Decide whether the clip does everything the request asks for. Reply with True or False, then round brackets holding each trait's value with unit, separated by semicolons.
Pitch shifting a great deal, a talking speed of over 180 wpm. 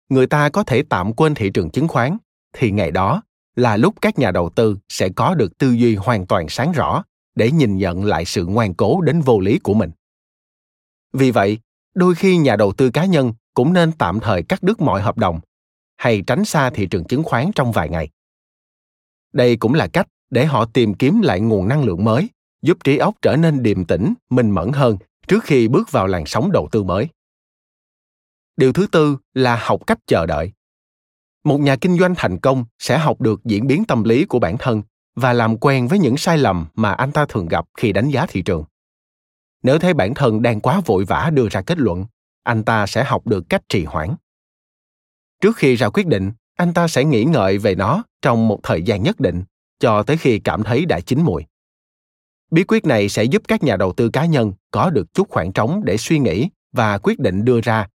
True (6.8 semitones; 220 wpm)